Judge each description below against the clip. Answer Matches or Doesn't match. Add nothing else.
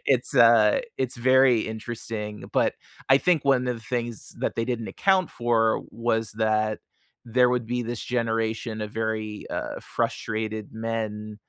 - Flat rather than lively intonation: Matches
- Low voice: Matches